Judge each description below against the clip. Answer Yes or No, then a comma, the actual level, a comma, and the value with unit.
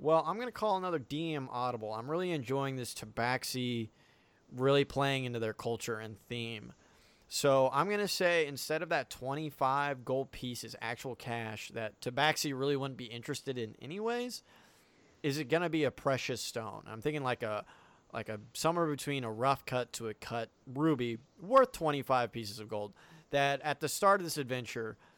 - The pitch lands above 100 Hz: Yes, low, 135 Hz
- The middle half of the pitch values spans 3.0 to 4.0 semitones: No, average, 4.8 semitones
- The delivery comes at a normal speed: Yes, average, 180 wpm